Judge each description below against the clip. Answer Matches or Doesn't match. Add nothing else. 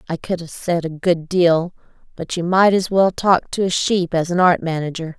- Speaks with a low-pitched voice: Doesn't match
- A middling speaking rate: Doesn't match